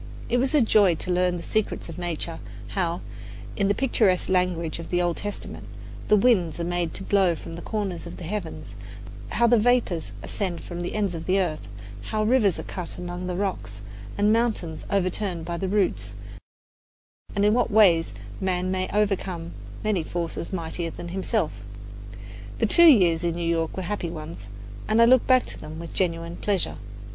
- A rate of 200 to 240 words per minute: No, average, 190 wpm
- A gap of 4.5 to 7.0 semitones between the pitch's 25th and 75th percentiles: No, average, 3.6 semitones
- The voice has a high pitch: No, medium, 180 Hz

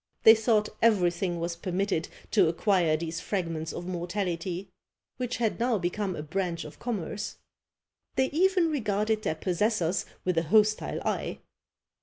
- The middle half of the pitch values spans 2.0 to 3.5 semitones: No, average, 4.1 semitones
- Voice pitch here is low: No, high, 190 Hz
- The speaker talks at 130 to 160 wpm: Yes, average, 140 wpm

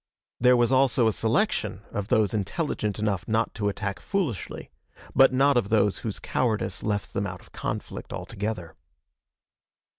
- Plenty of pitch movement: No, average, 3.5 semitones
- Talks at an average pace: Yes, average, 150 wpm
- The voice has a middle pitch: No, low, 110 Hz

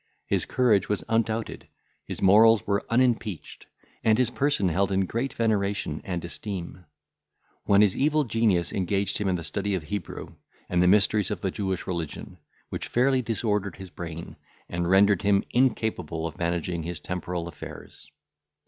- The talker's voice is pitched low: Yes, low, 100 Hz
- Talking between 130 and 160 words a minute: Yes, average, 155 wpm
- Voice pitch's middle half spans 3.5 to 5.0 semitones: Yes, average, 3.9 semitones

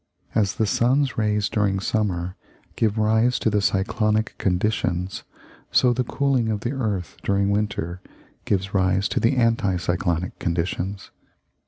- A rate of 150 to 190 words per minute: No, slow, 135 wpm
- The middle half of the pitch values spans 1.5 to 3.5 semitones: Yes, average, 3.0 semitones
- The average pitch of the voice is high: No, low, 105 Hz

